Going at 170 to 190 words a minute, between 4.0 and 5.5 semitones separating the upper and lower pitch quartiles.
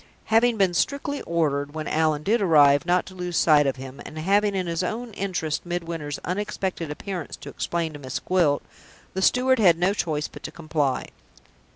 Yes: average, 185 wpm; average, 4.4 semitones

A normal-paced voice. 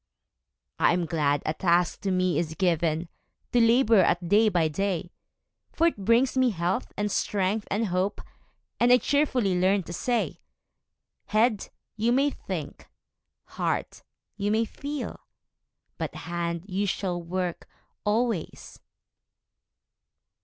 No: slow, 130 wpm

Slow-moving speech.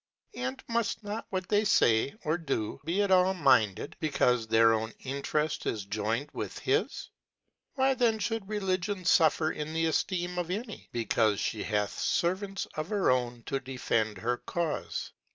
No: average, 155 wpm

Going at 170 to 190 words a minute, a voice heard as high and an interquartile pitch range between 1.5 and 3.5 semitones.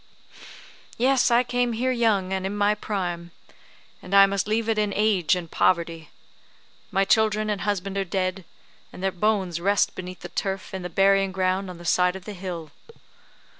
Yes: average, 180 wpm; high, 195 Hz; narrow, 2.6 semitones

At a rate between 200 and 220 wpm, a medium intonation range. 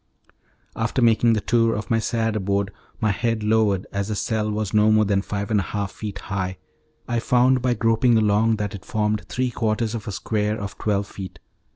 No: fast, 205 wpm; narrow, 1.9 semitones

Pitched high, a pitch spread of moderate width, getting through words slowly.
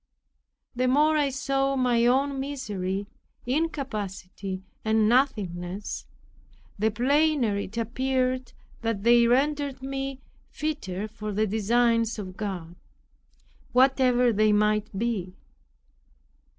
Yes: high, 235 Hz; average, 4.4 semitones; slow, 100 wpm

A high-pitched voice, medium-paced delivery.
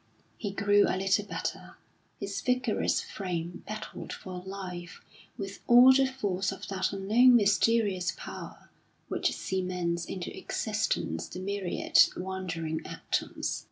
No: high, 195 Hz; slow, 125 wpm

